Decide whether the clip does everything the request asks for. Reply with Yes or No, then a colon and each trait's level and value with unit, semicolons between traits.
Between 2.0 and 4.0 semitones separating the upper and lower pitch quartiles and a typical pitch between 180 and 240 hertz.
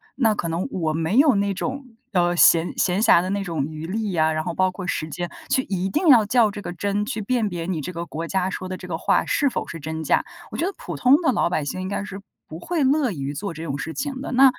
No: average, 5.2 semitones; medium, 185 Hz